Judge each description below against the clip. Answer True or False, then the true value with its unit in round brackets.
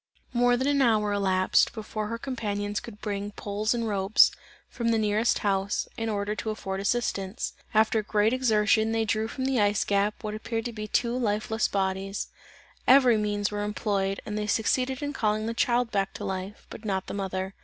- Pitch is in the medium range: False (215 Hz)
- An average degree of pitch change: False (2.2 semitones)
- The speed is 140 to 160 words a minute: False (190 wpm)